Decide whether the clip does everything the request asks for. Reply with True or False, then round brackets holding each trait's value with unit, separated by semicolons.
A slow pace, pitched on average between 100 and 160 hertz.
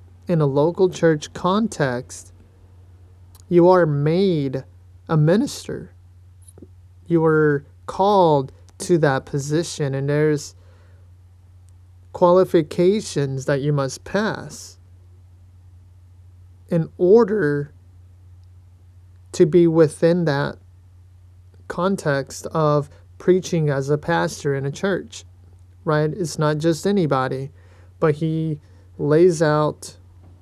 True (90 wpm; 135 Hz)